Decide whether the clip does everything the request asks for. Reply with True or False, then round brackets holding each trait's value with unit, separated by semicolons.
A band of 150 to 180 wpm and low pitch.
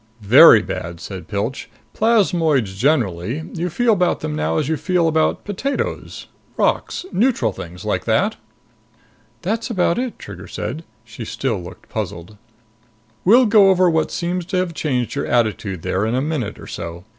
False (160 wpm; 145 Hz)